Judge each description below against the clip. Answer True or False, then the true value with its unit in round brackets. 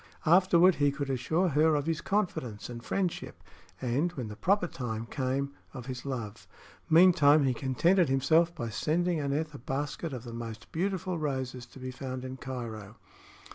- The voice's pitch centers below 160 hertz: True (140 Hz)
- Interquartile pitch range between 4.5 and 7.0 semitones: True (4.8 semitones)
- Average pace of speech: True (170 wpm)